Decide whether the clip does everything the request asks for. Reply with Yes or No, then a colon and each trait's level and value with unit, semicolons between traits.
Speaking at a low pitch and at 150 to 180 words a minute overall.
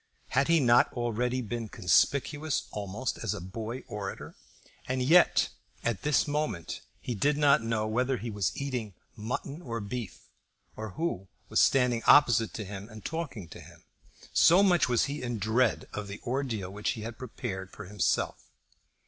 Yes: low, 120 Hz; average, 165 wpm